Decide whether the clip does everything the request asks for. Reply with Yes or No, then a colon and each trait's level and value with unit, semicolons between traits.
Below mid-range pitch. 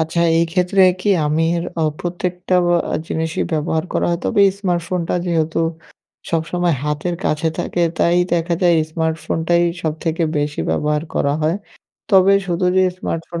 No: medium, 170 Hz